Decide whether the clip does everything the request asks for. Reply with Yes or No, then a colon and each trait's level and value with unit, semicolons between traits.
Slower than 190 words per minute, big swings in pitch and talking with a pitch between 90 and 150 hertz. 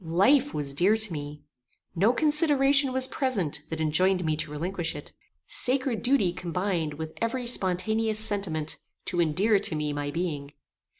No: average, 155 wpm; wide, 6.7 semitones; medium, 185 Hz